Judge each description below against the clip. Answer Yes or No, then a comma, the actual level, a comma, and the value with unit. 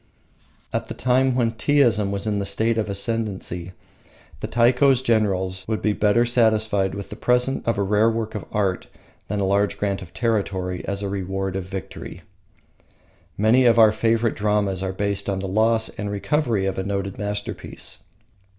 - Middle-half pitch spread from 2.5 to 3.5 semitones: Yes, average, 2.8 semitones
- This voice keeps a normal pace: Yes, average, 170 wpm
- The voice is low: Yes, low, 105 Hz